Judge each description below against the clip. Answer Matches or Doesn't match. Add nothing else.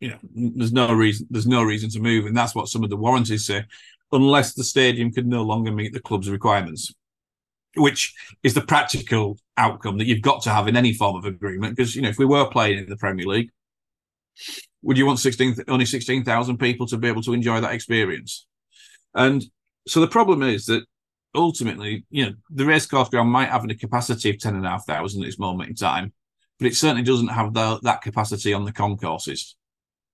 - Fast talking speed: Matches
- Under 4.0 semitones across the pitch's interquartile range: Matches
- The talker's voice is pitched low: Matches